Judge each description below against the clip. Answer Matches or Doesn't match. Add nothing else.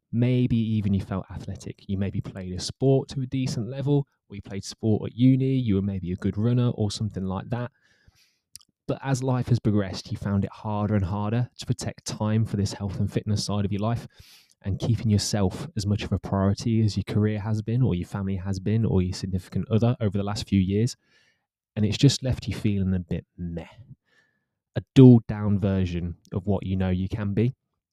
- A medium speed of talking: Doesn't match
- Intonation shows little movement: Doesn't match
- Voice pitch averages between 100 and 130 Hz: Matches